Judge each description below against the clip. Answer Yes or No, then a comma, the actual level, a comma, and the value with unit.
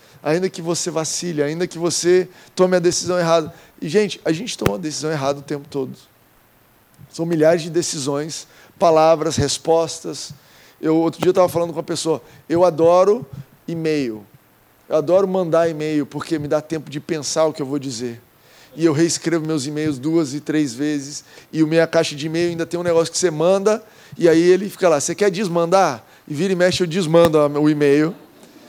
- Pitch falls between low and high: Yes, medium, 160 Hz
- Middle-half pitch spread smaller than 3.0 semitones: Yes, narrow, 2.5 semitones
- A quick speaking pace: Yes, fast, 195 wpm